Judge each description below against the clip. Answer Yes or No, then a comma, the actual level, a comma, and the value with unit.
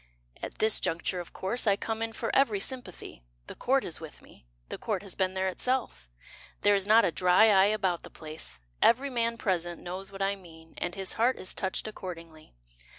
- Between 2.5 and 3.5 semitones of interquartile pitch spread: No, average, 4.1 semitones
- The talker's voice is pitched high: Yes, high, 195 Hz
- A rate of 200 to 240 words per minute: Yes, fast, 205 wpm